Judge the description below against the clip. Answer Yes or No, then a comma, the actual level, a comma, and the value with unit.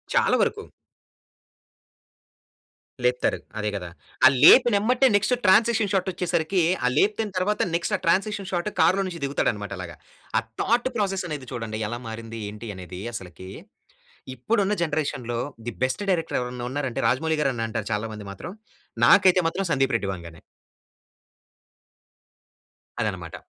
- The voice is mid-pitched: Yes, medium, 150 Hz